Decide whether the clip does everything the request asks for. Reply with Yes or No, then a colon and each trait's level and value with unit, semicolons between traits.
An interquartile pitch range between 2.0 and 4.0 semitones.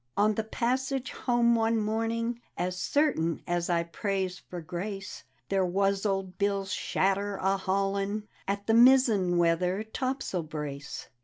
Yes: average, 3.7 semitones